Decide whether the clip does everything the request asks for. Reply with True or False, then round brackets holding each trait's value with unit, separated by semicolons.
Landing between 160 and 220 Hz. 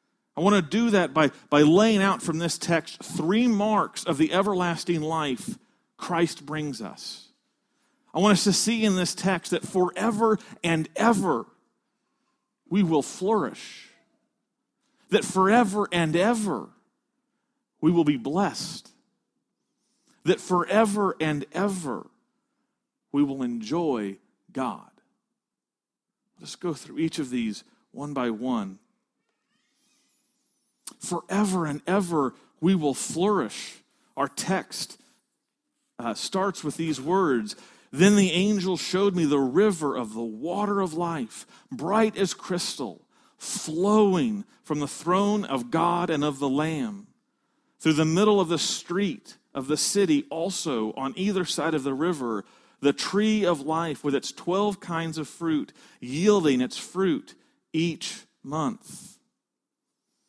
True (190 Hz)